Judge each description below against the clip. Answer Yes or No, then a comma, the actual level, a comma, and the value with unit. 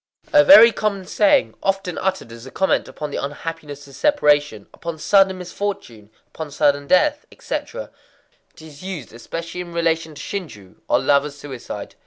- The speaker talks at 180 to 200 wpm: No, average, 155 wpm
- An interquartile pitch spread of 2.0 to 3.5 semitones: No, average, 5.2 semitones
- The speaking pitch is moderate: Yes, medium, 165 Hz